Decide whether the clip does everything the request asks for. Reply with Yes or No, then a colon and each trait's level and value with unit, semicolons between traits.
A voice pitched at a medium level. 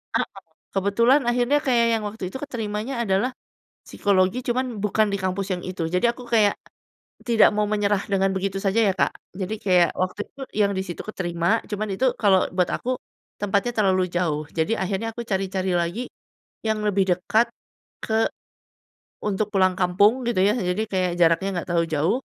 No: high, 200 Hz